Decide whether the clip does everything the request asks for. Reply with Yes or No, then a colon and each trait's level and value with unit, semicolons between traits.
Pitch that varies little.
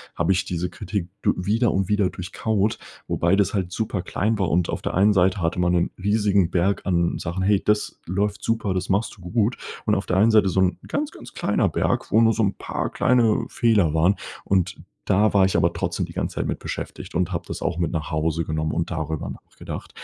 No: average, 3.3 semitones